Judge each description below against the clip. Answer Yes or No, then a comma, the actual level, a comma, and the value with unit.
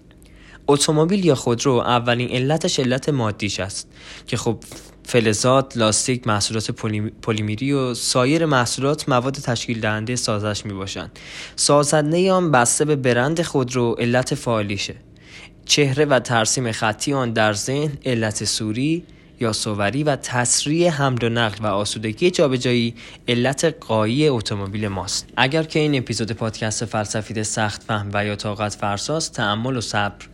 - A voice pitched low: Yes, low, 120 Hz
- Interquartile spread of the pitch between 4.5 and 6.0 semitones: Yes, average, 4.9 semitones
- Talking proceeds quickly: No, average, 135 wpm